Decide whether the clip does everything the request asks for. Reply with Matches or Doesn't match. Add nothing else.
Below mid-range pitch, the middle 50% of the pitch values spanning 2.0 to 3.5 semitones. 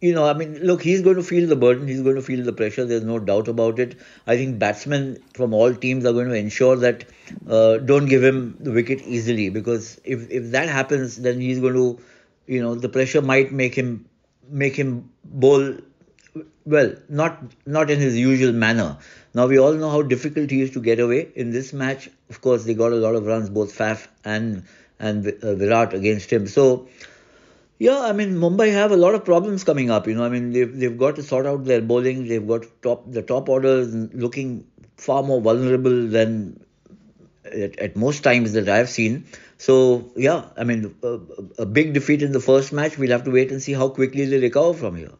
Matches